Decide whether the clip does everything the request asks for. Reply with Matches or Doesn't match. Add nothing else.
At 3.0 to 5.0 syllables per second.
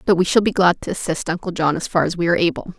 Doesn't match